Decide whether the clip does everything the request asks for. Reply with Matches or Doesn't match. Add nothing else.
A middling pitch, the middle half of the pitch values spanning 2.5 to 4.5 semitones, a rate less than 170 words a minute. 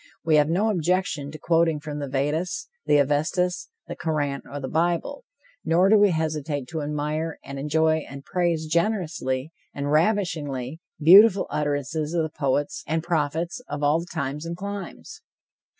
Matches